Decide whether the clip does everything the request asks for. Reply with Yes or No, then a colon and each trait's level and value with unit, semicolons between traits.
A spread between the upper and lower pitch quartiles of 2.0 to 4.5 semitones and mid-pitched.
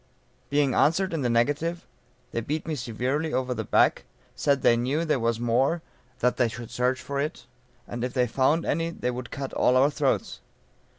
No: average, 3.8 semitones; low, 130 Hz